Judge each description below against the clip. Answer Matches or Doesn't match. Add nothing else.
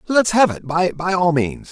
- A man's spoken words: Matches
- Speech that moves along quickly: Matches